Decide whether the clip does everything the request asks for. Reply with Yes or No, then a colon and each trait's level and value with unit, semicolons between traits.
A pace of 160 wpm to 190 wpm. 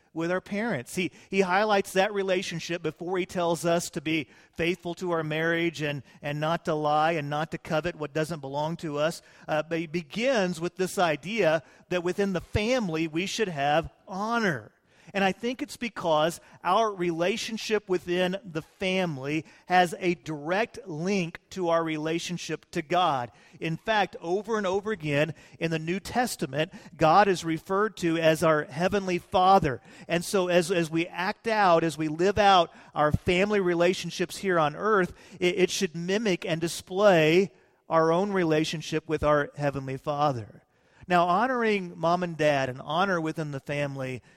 Yes: average, 170 wpm